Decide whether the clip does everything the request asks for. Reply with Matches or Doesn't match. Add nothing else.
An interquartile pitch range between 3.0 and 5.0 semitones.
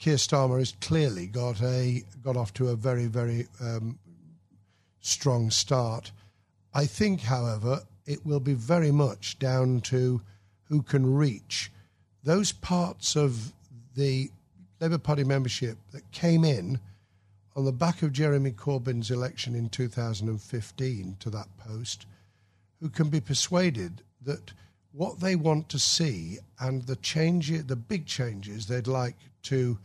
Doesn't match